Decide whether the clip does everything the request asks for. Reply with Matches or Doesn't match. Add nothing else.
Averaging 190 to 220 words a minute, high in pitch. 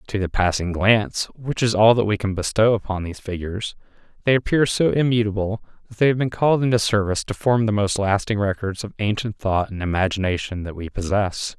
Doesn't match